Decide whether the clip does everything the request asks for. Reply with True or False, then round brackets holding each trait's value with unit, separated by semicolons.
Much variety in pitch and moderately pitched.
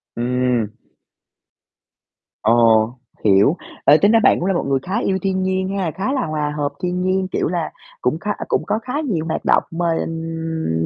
True (6.5 semitones; 165 Hz)